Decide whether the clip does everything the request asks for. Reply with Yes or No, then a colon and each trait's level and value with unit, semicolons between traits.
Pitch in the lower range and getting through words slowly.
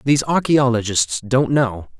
Yes: low, 130 Hz; slow, 120 wpm